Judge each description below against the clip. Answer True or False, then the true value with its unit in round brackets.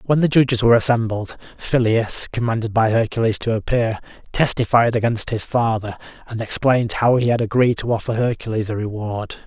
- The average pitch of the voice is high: False (115 Hz)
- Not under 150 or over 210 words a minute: True (165 wpm)